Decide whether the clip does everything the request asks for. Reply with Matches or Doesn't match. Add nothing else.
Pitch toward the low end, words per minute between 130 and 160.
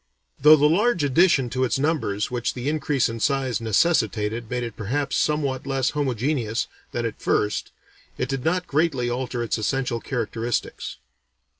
Matches